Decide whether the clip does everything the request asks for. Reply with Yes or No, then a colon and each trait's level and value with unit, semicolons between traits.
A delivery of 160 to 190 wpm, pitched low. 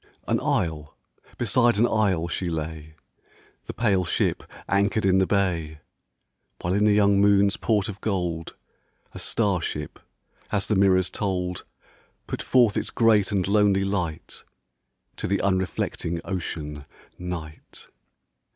No: average, 140 wpm; very low, 95 Hz